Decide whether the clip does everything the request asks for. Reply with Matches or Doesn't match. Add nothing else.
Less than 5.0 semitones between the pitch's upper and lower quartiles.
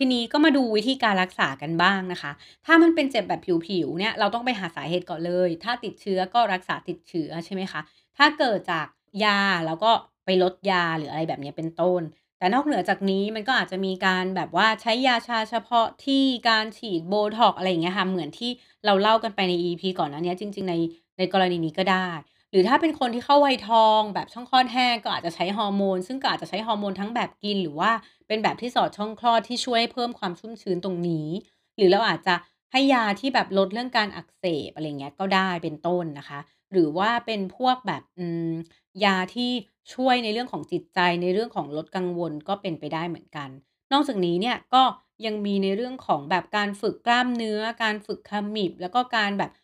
Matches